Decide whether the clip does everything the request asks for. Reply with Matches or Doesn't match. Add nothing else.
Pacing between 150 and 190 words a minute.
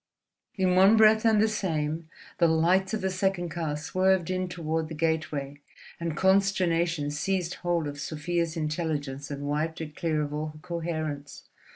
Matches